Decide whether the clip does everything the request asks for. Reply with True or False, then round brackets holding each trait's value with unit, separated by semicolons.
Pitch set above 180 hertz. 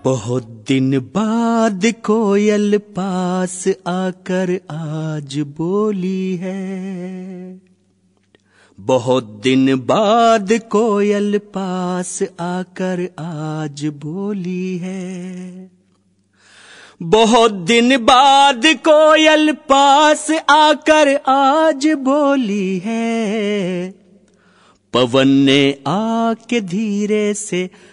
True (190 Hz)